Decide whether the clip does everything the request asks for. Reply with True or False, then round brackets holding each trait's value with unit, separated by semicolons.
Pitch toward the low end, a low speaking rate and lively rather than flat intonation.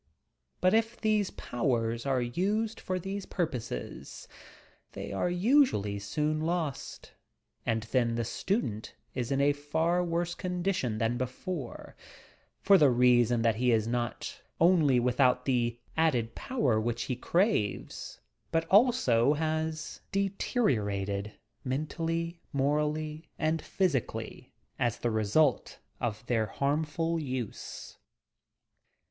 False (145 Hz; 120 wpm; 6.4 semitones)